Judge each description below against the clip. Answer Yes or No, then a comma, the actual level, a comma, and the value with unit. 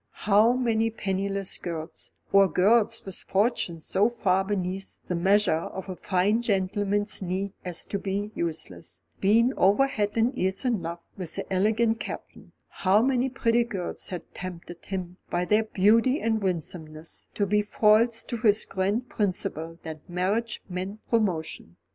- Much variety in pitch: No, average, 3.5 semitones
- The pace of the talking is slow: No, average, 155 wpm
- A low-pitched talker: No, high, 195 Hz